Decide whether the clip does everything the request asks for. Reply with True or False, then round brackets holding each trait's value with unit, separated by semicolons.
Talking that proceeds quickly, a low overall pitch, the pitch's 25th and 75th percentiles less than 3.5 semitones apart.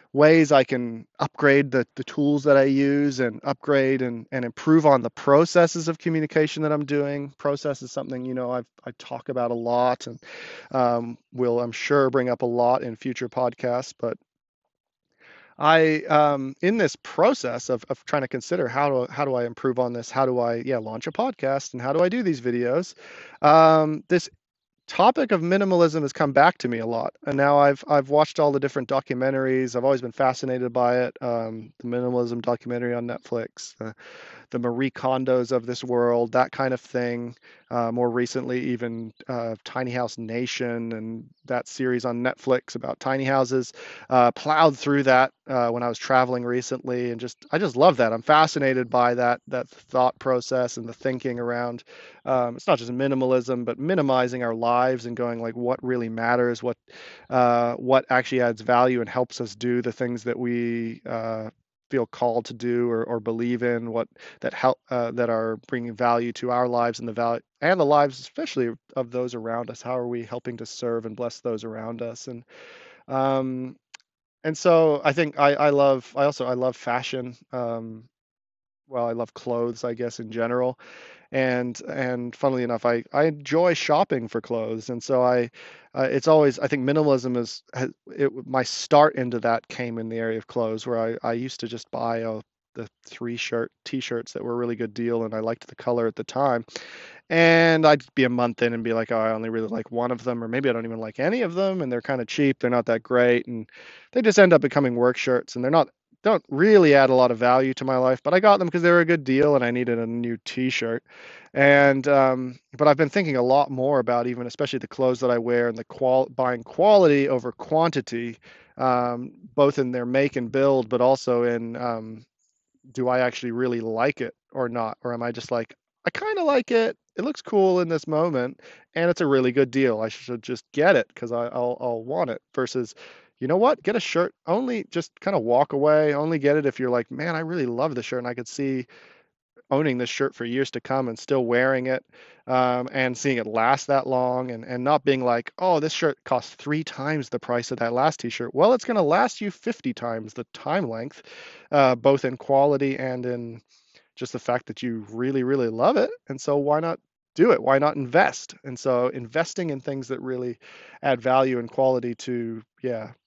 True (210 wpm; 125 Hz; 2.8 semitones)